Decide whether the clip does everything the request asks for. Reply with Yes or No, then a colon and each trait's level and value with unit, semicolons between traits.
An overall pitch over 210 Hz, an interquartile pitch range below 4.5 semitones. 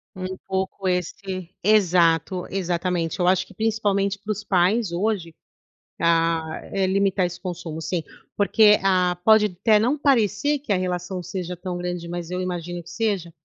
No: medium, 185 Hz; narrow, 2.5 semitones